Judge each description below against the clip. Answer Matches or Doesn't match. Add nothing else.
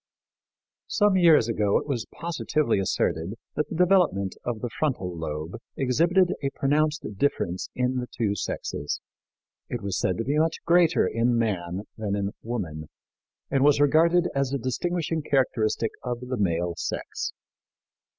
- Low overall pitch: Matches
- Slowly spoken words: Doesn't match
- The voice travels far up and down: Matches